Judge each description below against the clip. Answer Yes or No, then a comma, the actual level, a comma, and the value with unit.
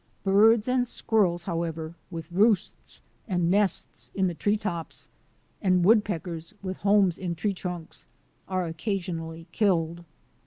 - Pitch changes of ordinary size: Yes, average, 3.4 semitones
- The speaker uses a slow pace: Yes, slow, 130 wpm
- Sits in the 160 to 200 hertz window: Yes, medium, 185 Hz